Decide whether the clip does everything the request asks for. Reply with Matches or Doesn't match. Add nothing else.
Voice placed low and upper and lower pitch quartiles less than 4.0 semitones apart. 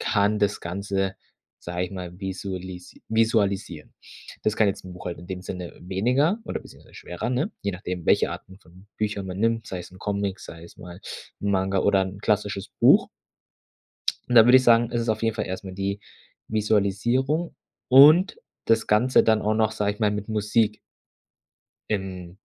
Matches